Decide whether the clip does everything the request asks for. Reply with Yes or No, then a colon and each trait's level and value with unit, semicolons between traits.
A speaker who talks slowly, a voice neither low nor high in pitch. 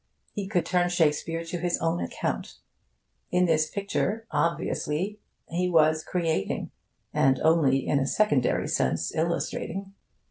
Yes: slow, 130 wpm; medium, 170 Hz